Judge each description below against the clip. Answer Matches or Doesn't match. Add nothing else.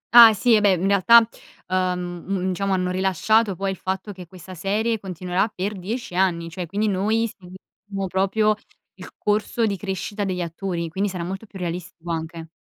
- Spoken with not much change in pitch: Matches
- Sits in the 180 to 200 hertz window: Matches